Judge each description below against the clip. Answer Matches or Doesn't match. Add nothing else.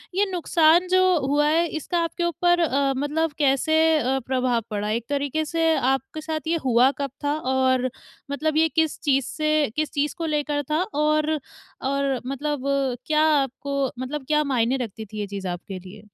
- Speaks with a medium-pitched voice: Doesn't match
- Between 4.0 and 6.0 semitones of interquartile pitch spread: Doesn't match